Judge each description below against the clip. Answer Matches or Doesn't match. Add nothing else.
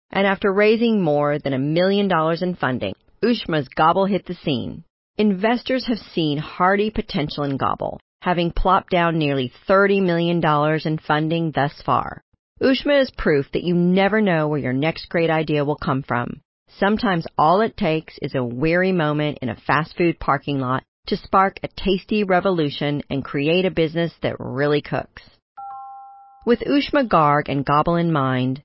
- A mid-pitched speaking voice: Matches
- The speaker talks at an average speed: Matches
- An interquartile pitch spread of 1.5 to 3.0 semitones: Doesn't match